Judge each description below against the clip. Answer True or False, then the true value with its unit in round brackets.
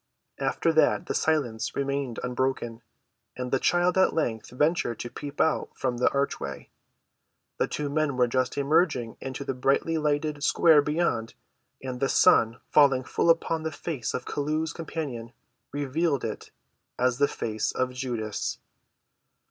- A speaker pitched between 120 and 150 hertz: True (140 Hz)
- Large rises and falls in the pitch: False (3.8 semitones)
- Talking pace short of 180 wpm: True (150 wpm)